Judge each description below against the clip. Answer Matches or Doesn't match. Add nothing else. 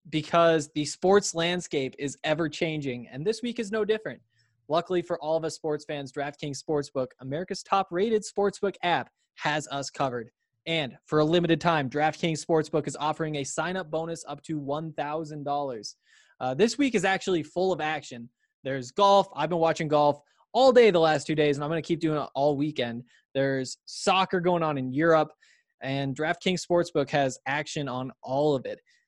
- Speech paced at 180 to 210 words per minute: Matches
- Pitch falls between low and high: Matches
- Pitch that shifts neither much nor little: Matches